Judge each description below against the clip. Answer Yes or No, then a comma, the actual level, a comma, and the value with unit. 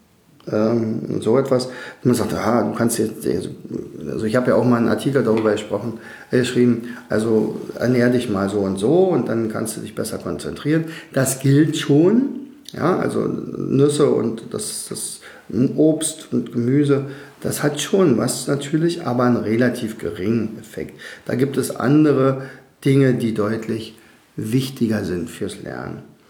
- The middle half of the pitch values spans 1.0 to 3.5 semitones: No, average, 4.1 semitones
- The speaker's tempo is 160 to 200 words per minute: No, average, 150 wpm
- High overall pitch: No, low, 125 Hz